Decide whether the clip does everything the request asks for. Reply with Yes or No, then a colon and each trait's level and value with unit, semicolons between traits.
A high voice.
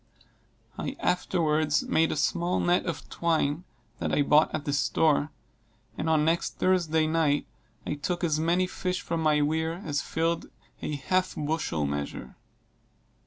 No: medium, 160 Hz